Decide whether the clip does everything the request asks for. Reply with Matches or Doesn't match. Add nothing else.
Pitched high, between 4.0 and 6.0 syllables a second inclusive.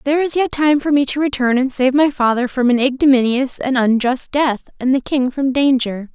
Matches